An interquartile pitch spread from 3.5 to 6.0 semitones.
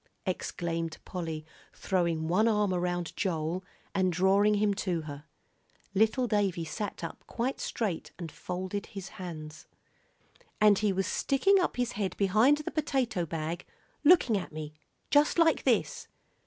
Yes: average, 4.2 semitones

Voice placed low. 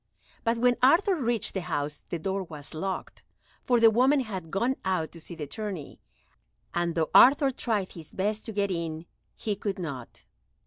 No: high, 195 Hz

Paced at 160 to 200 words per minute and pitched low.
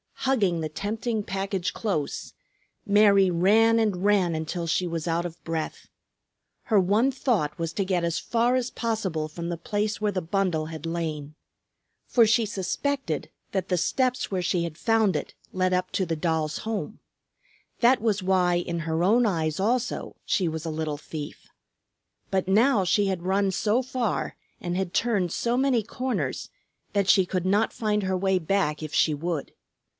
No: average, 175 wpm; high, 190 Hz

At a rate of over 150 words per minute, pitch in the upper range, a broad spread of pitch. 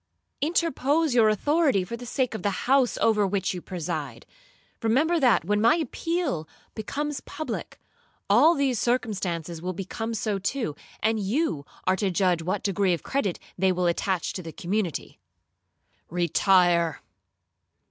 No: average, 145 wpm; high, 210 Hz; wide, 6.3 semitones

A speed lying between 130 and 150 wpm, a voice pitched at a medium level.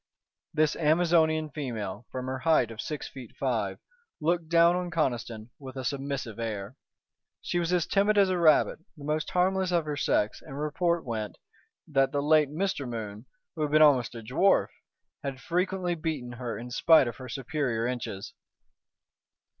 No: average, 170 wpm; medium, 145 Hz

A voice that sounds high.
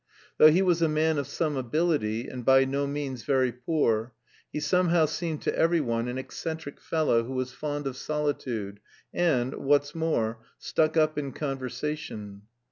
No: medium, 145 Hz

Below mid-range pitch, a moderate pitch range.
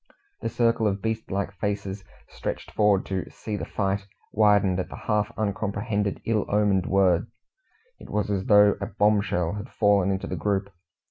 No: low, 100 Hz; narrow, 1.3 semitones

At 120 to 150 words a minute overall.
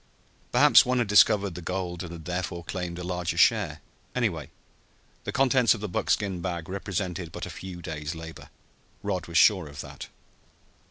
No: average, 170 wpm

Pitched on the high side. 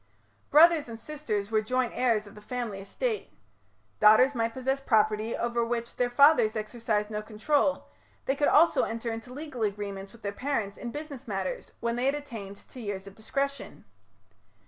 Yes: high, 230 Hz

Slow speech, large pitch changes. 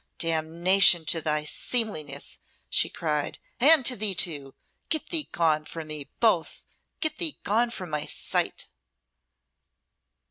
Yes: slow, 130 wpm; wide, 7.0 semitones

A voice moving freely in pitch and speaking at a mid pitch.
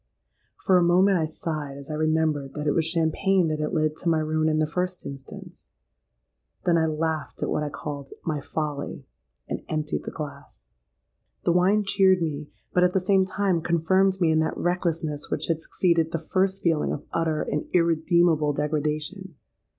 No: average, 2.8 semitones; medium, 160 Hz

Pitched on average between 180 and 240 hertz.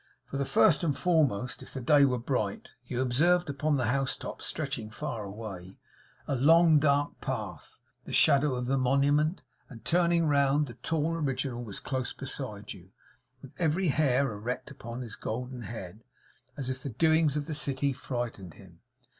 No: low, 135 Hz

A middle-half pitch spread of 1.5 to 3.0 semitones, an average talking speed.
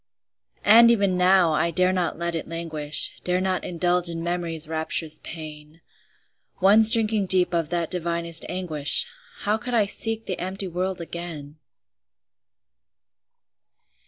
No: narrow, 2.5 semitones; slow, 130 wpm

